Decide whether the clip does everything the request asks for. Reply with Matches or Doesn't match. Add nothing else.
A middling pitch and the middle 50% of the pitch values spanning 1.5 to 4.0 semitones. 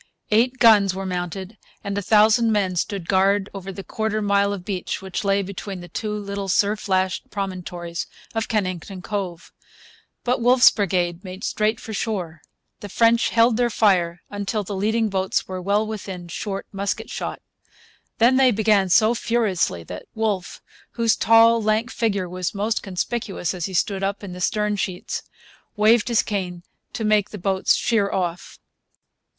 Doesn't match